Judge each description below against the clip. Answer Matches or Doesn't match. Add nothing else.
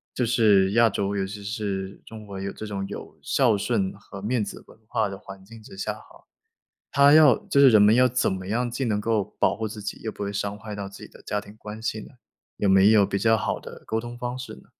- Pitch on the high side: Doesn't match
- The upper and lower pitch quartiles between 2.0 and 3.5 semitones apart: Matches